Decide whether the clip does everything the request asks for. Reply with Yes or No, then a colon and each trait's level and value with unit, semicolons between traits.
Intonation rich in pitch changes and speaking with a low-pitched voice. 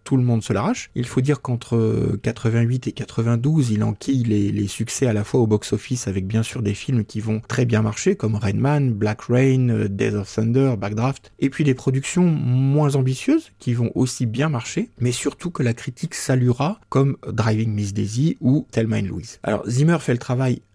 No: average, 3.7 semitones; low, 120 Hz